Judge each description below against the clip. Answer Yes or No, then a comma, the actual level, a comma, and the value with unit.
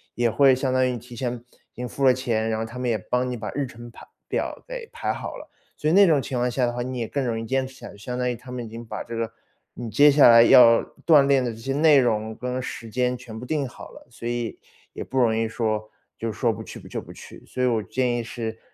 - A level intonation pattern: Yes, narrow, 2.2 semitones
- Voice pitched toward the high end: No, low, 125 Hz